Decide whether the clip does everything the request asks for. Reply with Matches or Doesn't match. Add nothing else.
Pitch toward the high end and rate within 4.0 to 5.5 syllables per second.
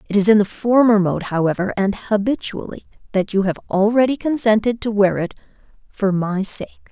Matches